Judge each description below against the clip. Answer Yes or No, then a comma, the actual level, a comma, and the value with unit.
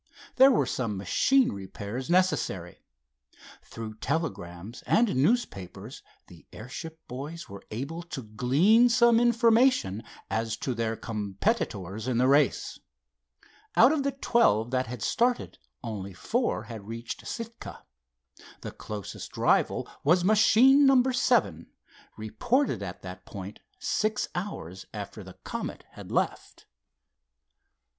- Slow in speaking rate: Yes, slow, 120 wpm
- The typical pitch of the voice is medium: No, low, 130 Hz